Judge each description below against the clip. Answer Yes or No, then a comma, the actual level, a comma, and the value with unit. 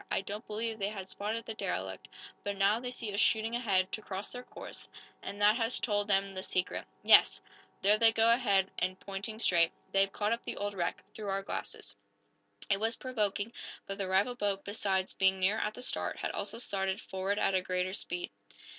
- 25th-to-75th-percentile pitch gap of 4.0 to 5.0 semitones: No, narrow, 2.6 semitones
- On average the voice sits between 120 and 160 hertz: No, high, 205 Hz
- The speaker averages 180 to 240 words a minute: Yes, average, 200 wpm